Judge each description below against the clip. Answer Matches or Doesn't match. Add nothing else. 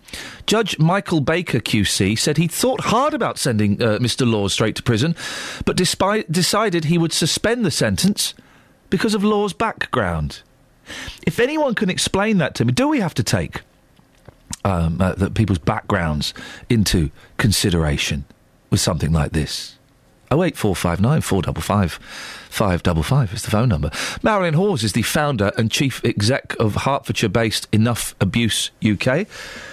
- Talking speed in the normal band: Matches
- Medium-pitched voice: Doesn't match